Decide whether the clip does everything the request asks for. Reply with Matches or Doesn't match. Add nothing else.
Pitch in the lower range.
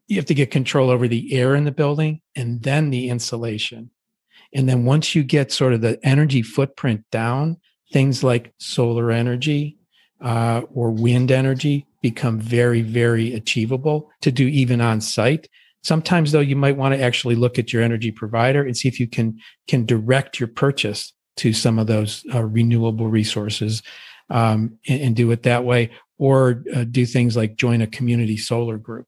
Matches